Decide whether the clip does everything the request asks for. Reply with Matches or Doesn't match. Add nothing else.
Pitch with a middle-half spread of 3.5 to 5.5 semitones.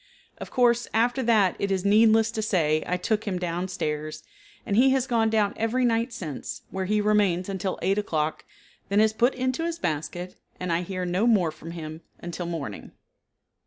Matches